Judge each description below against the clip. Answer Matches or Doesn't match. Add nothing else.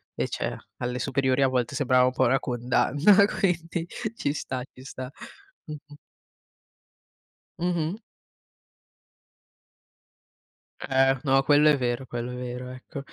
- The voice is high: Doesn't match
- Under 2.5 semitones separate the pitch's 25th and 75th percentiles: Doesn't match